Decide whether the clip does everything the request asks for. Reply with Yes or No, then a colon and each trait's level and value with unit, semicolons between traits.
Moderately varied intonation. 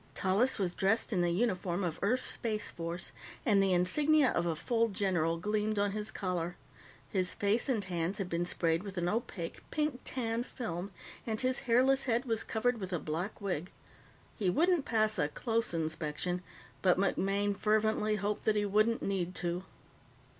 Yes: average, 4.2 semitones